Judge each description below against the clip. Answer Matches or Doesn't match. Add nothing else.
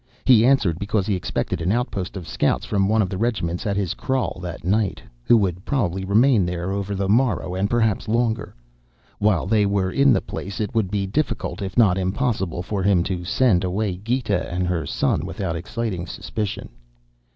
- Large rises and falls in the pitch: Doesn't match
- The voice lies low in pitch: Matches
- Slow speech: Doesn't match